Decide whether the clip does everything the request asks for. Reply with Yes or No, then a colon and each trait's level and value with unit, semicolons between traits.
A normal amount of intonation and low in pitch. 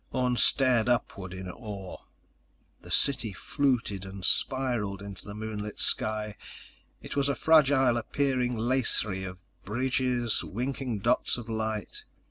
Yes: average, 4.0 semitones; low, 115 Hz